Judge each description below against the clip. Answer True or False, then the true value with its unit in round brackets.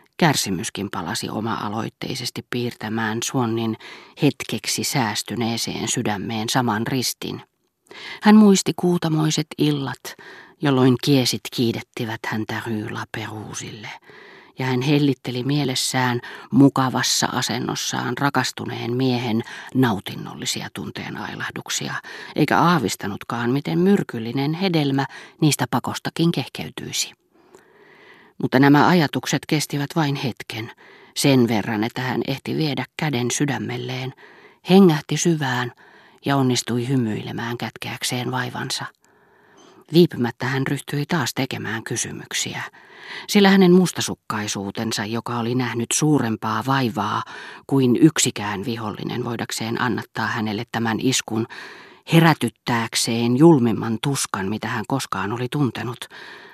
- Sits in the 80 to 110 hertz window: False (125 Hz)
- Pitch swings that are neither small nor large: True (3.6 semitones)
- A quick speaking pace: False (95 wpm)